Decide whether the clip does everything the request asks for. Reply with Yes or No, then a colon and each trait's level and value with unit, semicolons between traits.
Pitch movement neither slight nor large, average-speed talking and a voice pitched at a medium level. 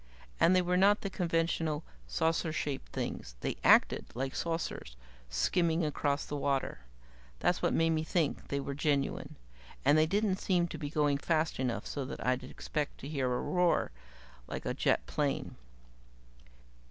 Yes: average, 3.3 semitones; average, 165 wpm; medium, 155 Hz